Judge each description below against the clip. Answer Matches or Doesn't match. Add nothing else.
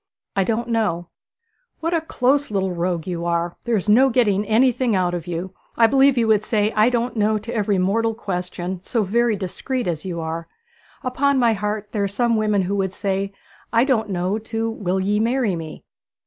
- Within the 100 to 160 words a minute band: Doesn't match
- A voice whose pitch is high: Matches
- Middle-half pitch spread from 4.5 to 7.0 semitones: Doesn't match